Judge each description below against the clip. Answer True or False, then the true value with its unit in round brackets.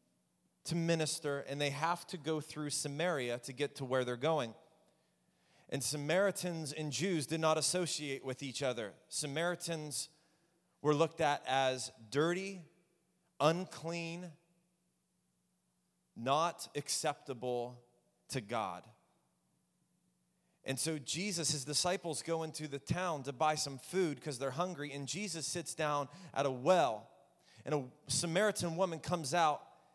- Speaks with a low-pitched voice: False (155 Hz)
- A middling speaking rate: False (130 wpm)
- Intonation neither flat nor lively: True (3.8 semitones)